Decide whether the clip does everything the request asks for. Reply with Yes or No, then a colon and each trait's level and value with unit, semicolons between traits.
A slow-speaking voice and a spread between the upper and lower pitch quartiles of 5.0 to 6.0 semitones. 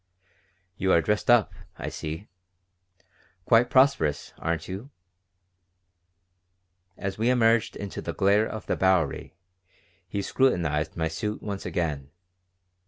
Yes: slow, 115 wpm; wide, 5.5 semitones